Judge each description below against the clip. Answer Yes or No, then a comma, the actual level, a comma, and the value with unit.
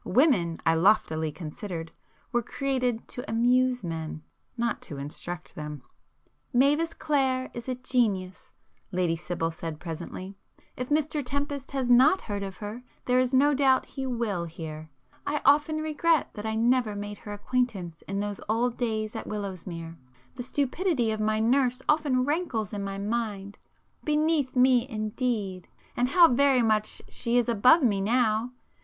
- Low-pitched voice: No, high, 235 Hz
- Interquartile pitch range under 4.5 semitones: No, average, 5.0 semitones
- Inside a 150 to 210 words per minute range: No, average, 140 wpm